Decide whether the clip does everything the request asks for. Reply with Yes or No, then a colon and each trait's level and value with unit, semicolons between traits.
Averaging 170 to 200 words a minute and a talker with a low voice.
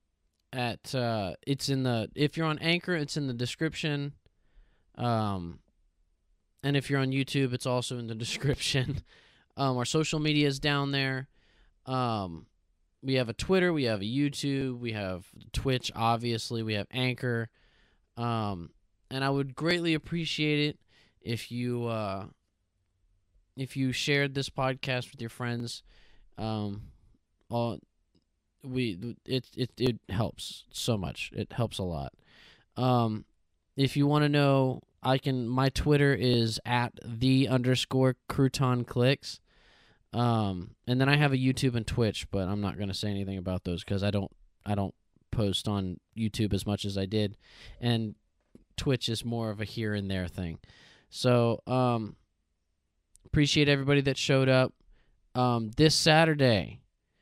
No: average, 150 wpm; low, 120 Hz